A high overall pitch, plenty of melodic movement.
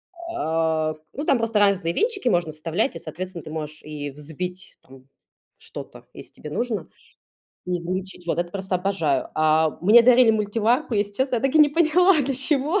Yes: high, 195 Hz; wide, 7.8 semitones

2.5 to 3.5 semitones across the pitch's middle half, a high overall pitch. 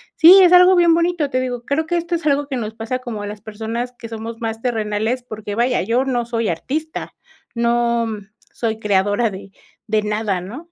No: average, 4.3 semitones; high, 235 Hz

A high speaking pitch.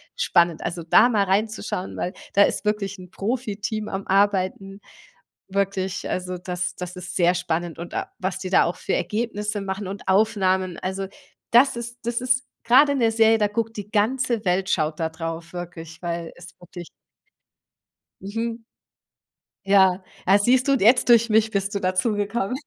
Yes: high, 195 Hz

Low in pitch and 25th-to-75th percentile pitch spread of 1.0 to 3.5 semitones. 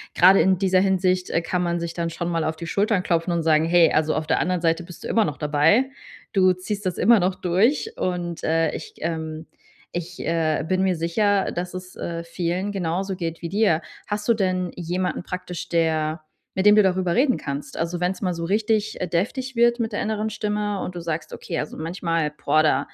No: medium, 180 Hz; average, 2.8 semitones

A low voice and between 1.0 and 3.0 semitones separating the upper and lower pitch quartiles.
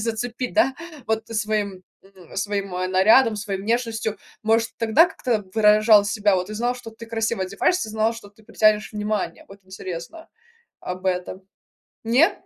No: high, 215 Hz; narrow, 2.4 semitones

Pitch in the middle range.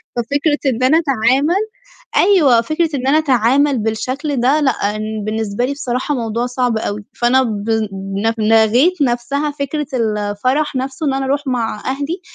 No: very high, 255 Hz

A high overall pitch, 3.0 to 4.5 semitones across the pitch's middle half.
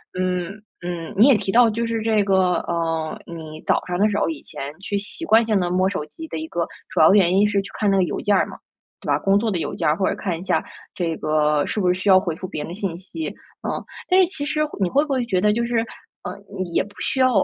Yes: high, 195 Hz; average, 4.1 semitones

